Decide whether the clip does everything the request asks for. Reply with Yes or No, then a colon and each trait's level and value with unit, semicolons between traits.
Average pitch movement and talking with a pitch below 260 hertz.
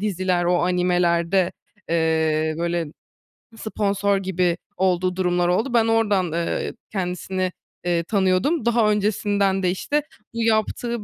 Yes: average, 3.0 semitones; medium, 185 Hz